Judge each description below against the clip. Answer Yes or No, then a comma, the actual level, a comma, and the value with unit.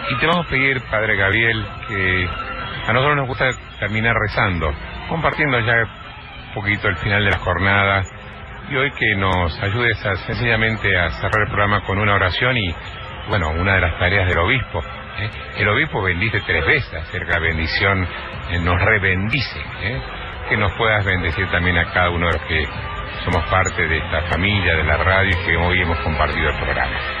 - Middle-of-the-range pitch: No, very low, 95 Hz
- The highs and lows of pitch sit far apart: No, average, 4.0 semitones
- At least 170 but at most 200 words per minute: Yes, average, 185 wpm